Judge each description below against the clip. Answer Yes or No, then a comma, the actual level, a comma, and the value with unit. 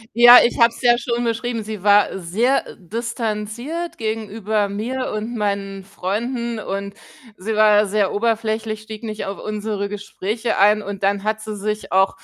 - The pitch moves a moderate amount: No, narrow, 2.3 semitones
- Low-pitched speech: No, high, 215 Hz